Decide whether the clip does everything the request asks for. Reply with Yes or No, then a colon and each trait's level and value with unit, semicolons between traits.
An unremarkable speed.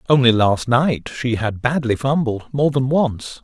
Yes: average, 175 wpm